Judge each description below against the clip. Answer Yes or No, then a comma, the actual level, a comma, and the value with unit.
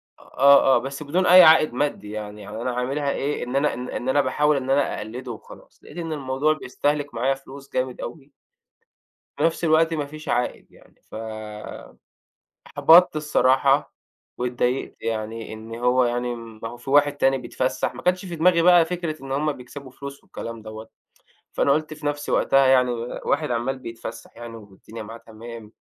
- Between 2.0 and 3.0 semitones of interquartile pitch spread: No, average, 4.0 semitones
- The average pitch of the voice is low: Yes, low, 130 Hz